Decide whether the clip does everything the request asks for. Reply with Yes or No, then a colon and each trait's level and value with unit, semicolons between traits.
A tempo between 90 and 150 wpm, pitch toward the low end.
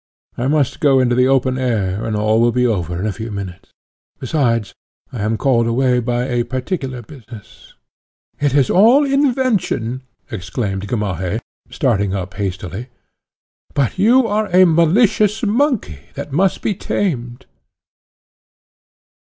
Yes: slow, 135 wpm; low, 125 Hz